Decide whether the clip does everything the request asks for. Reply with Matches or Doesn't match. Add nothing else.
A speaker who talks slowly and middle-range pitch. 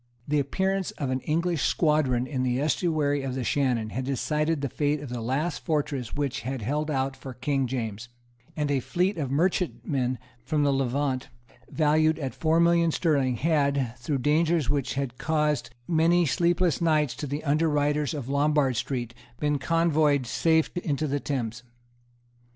Doesn't match